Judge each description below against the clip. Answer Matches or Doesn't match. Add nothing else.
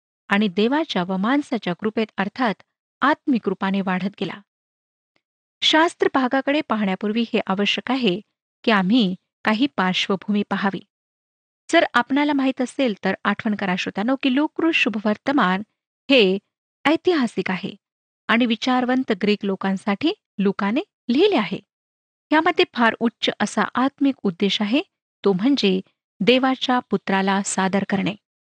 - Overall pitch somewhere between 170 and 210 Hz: Doesn't match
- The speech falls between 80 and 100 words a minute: Doesn't match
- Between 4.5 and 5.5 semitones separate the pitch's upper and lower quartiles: Matches